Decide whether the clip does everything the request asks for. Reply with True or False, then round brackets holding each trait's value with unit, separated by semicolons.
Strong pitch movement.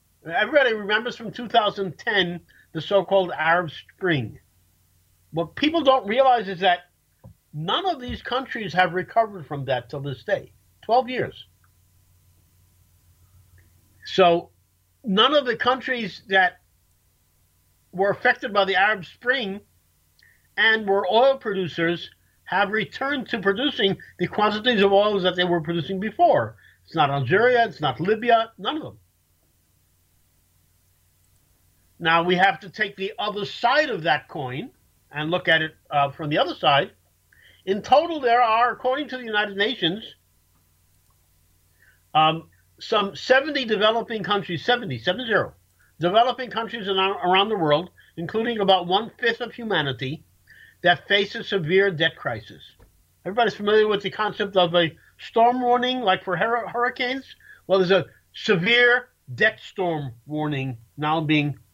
True (9.0 semitones)